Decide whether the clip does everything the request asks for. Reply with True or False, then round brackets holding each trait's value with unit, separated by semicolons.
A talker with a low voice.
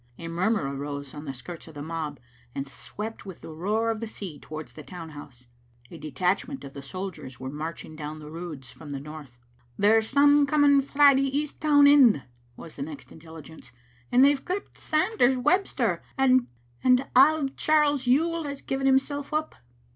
False (210 Hz)